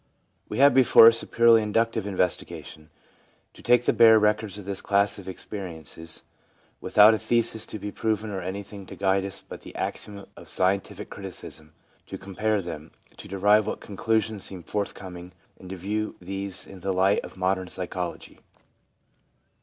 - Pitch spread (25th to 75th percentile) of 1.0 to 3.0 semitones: Yes, narrow, 2.6 semitones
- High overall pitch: No, low, 100 Hz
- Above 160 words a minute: Yes, average, 170 wpm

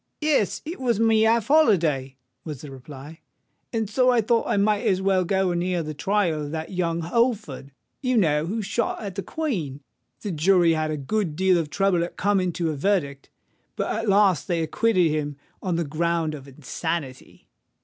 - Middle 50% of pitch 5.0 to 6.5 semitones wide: Yes, average, 5.3 semitones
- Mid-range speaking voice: Yes, medium, 180 Hz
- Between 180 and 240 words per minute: Yes, average, 190 wpm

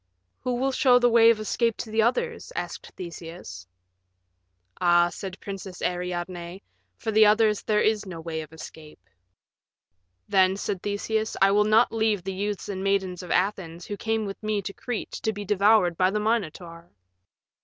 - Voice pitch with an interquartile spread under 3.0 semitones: No, average, 3.5 semitones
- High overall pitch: Yes, high, 200 Hz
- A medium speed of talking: Yes, average, 175 wpm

